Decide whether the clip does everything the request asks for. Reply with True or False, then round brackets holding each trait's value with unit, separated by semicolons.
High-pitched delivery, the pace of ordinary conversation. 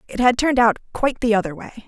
False (230 Hz; 255 wpm)